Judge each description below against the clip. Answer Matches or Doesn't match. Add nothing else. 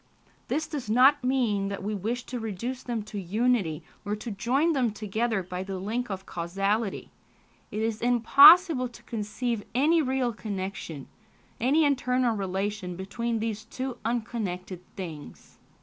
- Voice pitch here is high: Matches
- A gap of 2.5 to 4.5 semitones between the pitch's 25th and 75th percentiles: Matches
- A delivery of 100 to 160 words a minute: Matches